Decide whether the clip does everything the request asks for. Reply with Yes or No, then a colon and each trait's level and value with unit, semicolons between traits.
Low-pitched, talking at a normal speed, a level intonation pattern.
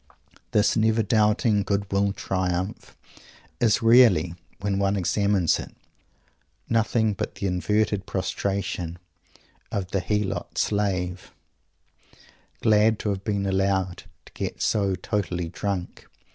No: low, 100 Hz; slow, 115 wpm; narrow, 2.1 semitones